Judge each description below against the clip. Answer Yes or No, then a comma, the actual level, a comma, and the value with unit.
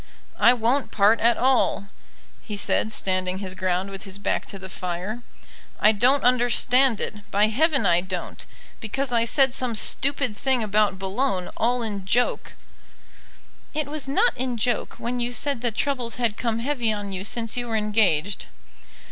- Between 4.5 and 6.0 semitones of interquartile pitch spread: No, average, 3.9 semitones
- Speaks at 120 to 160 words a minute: No, average, 175 wpm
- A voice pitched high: Yes, high, 225 Hz